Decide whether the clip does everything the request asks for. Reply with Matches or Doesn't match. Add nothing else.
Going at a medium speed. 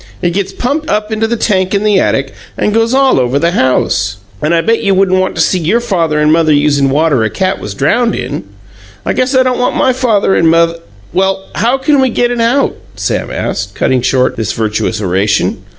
Doesn't match